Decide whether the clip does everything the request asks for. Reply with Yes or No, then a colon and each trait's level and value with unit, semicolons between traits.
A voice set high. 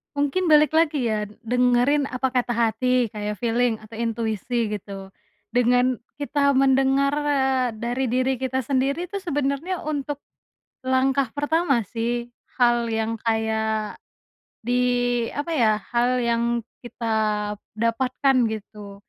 Yes: high, 245 Hz